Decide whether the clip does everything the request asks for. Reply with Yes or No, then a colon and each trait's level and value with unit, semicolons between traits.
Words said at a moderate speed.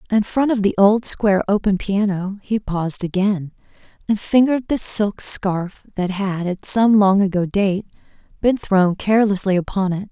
Yes: average, 165 wpm